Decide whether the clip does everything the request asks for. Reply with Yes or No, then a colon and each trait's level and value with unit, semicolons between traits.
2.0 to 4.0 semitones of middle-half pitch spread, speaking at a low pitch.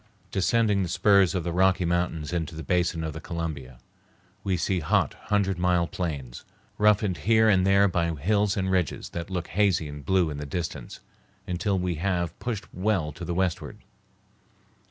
Yes: average, 2.9 semitones; very low, 90 Hz